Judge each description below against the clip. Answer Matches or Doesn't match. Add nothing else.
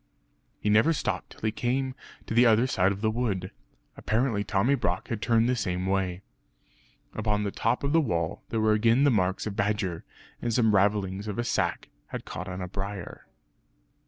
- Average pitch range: Matches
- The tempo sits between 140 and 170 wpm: Doesn't match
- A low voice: Matches